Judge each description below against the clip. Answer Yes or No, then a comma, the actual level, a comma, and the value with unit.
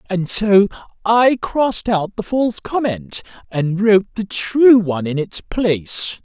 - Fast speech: No, average, 155 wpm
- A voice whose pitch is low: No, high, 200 Hz